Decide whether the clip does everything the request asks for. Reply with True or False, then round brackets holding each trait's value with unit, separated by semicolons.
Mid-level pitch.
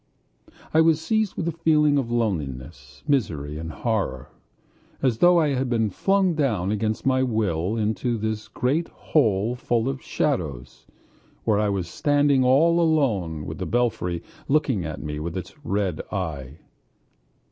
False (110 Hz)